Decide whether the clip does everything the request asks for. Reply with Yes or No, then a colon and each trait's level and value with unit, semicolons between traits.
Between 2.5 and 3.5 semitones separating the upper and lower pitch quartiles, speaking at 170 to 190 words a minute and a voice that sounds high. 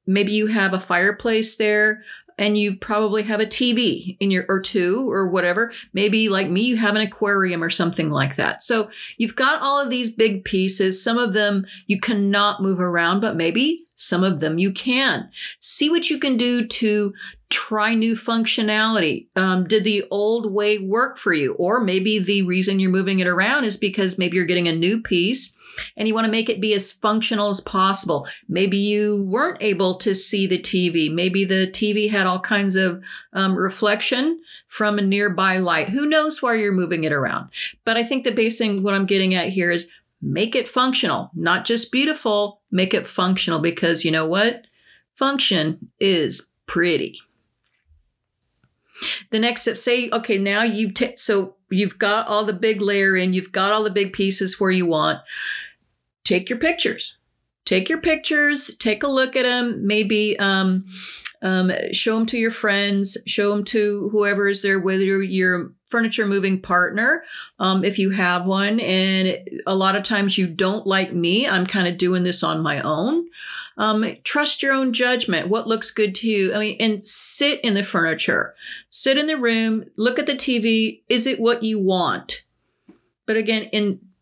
Yes: average, 3.0 semitones; average, 185 wpm; high, 205 Hz